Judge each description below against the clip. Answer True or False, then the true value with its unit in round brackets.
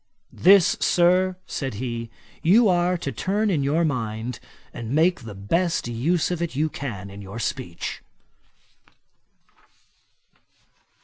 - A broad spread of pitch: True (7.3 semitones)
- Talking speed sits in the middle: False (125 wpm)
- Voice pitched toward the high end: False (145 Hz)